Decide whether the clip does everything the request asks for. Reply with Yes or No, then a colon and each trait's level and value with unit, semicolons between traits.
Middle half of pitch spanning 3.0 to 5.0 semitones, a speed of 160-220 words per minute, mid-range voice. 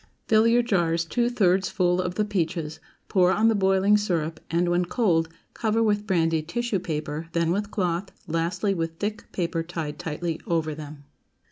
Yes: average, 3.9 semitones; average, 170 wpm; medium, 180 Hz